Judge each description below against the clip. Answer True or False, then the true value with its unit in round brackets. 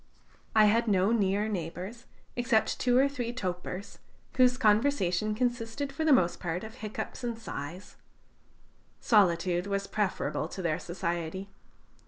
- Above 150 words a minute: False (135 wpm)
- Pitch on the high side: True (210 Hz)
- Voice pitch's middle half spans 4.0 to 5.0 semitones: True (4.7 semitones)